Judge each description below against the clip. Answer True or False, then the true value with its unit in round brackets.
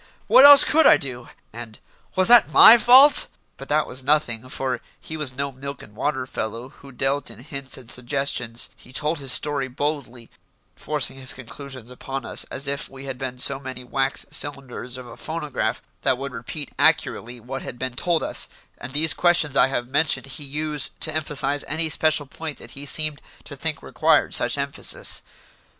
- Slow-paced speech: False (185 wpm)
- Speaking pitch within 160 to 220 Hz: False (135 Hz)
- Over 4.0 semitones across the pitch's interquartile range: False (2.9 semitones)